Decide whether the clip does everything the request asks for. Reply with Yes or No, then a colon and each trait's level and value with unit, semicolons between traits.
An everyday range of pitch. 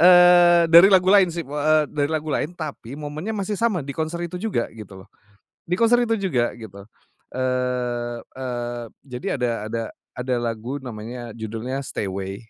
No: wide, 6.4 semitones